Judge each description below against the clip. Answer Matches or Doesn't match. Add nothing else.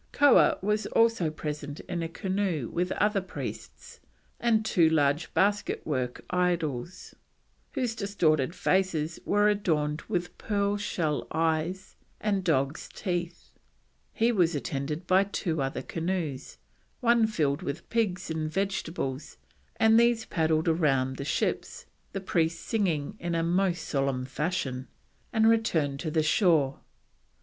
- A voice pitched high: Doesn't match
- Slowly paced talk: Matches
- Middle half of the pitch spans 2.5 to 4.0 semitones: Doesn't match